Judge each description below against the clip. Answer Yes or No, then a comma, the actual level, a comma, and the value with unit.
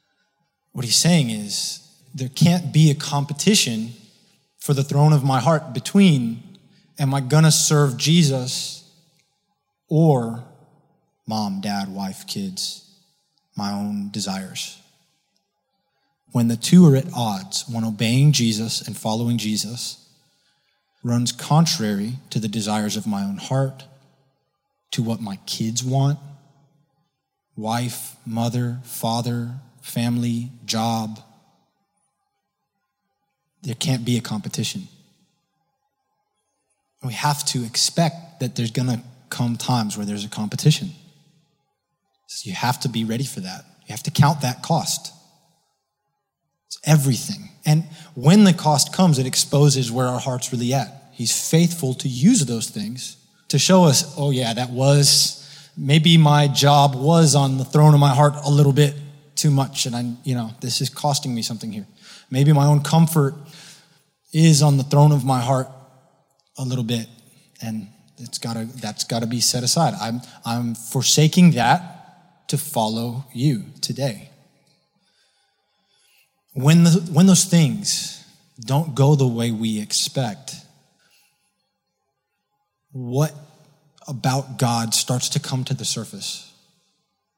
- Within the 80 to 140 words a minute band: Yes, slow, 135 wpm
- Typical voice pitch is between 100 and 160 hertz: Yes, medium, 140 Hz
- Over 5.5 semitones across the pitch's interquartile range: No, average, 5.2 semitones